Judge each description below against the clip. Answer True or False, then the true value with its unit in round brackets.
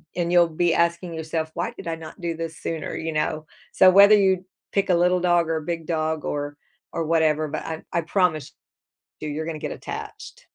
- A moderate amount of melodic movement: False (1.8 semitones)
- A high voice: False (165 Hz)